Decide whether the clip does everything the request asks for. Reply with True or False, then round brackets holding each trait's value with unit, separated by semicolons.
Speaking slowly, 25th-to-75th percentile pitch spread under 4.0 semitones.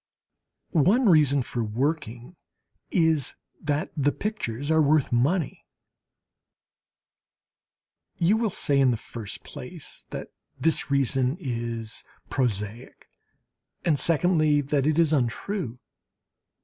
False (105 wpm; 4.8 semitones)